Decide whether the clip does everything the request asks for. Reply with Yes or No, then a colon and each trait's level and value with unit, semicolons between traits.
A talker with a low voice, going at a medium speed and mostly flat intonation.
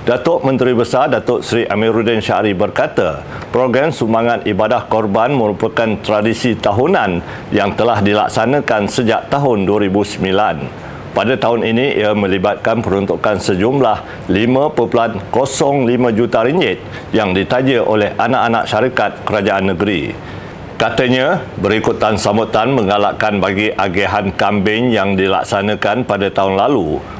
No: low, 105 Hz; average, 110 wpm; average, 3.0 semitones